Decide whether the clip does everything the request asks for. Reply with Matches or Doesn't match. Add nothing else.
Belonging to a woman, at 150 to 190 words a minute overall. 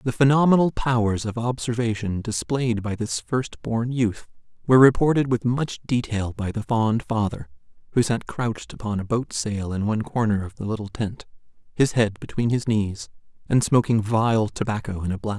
Doesn't match